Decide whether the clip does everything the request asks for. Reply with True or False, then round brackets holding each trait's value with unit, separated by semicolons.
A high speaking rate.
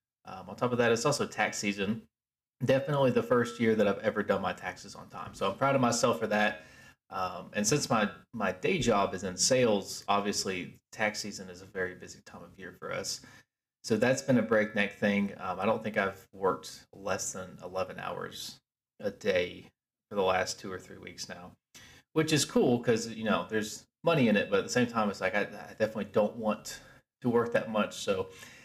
True (215 wpm)